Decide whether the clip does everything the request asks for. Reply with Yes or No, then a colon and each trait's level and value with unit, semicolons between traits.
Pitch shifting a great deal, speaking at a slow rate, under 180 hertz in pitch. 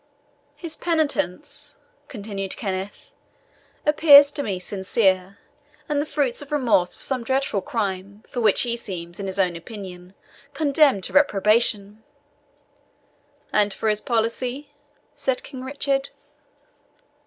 No: wide, 6.4 semitones; slow, 120 wpm; high, 225 Hz